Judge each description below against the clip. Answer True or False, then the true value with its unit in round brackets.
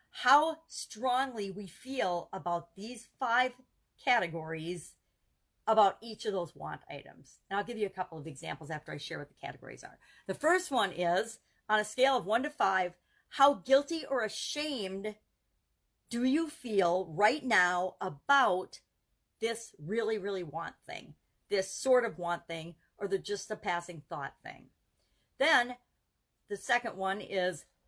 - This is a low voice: False (205 Hz)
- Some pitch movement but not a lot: False (5.7 semitones)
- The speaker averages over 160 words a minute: False (155 wpm)